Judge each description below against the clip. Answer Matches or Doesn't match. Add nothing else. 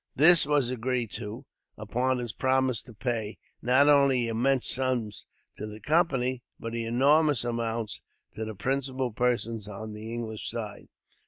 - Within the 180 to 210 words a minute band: Doesn't match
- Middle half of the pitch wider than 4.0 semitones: Doesn't match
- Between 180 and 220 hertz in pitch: Doesn't match